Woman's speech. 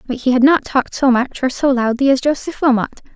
Yes: female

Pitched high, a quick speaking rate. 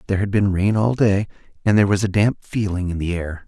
No: low, 100 Hz; fast, 260 wpm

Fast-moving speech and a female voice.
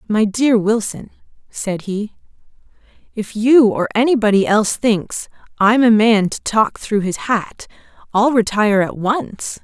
No: average, 145 wpm; female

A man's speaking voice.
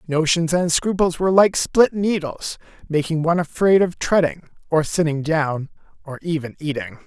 Yes: male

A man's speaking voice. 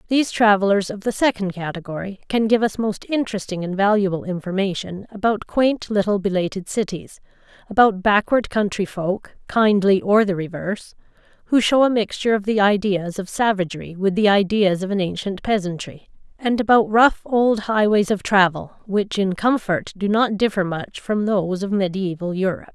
No: female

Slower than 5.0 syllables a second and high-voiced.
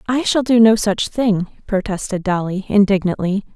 Yes: 4.6 syllables/s; high, 205 Hz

